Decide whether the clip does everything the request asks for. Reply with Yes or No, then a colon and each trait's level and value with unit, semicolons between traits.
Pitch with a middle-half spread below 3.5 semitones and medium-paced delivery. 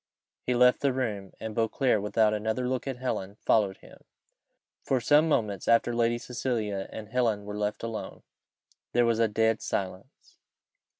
Yes: average, 3.1 semitones; average, 160 wpm